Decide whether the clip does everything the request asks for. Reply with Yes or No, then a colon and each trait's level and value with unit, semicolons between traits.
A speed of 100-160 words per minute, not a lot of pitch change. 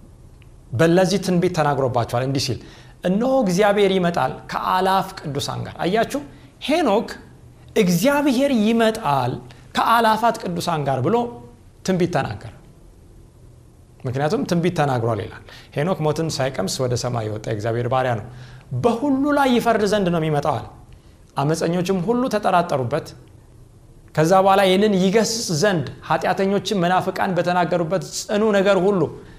No: fast, 110 wpm; wide, 8.1 semitones